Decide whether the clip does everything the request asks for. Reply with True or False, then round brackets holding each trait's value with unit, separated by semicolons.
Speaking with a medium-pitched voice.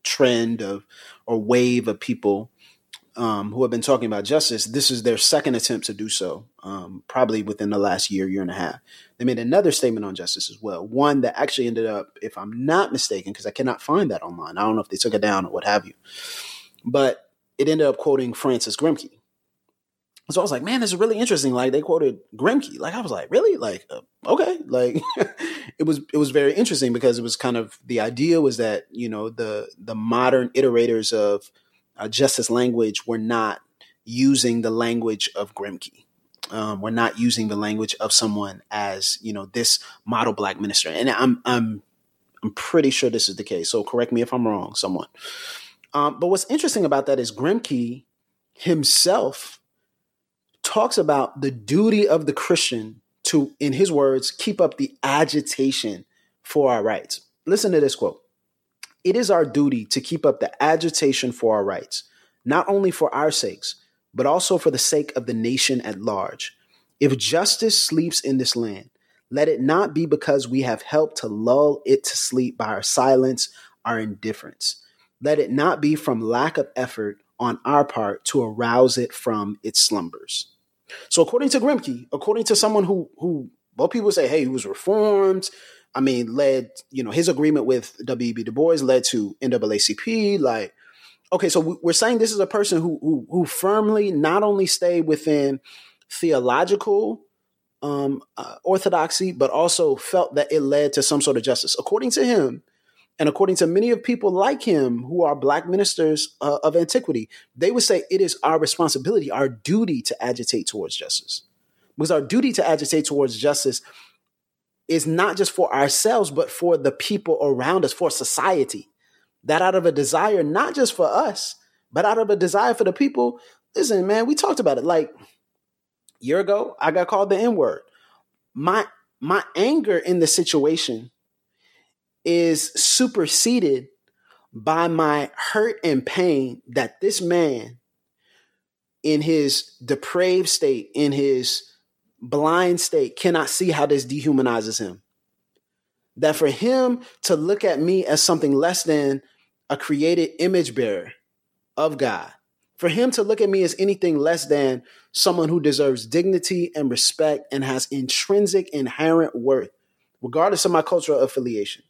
True (150 Hz)